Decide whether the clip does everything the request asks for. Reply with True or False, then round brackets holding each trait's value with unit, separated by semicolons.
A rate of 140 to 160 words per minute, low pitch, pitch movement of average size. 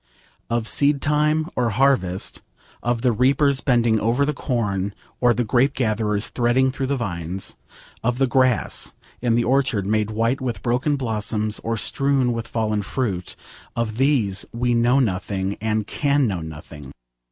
True (155 wpm; 120 Hz; 3.7 semitones)